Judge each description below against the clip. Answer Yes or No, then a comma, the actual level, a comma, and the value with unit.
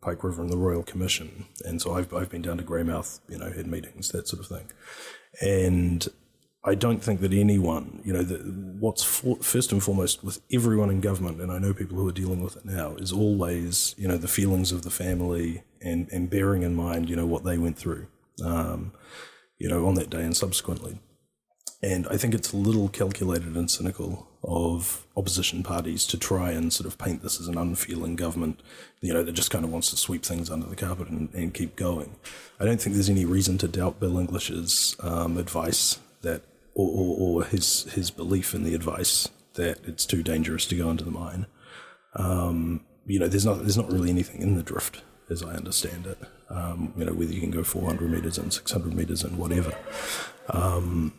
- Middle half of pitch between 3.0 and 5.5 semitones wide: No, narrow, 2.5 semitones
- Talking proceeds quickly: Yes, fast, 210 wpm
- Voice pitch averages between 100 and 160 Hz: No, very low, 90 Hz